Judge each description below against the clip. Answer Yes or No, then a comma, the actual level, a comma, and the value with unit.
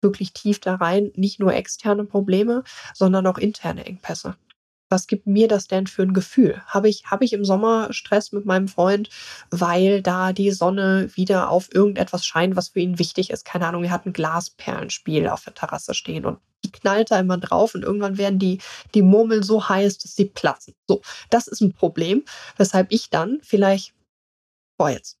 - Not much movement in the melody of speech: Yes, narrow, 2.1 semitones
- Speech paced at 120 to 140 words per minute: No, fast, 190 wpm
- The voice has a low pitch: No, high, 195 Hz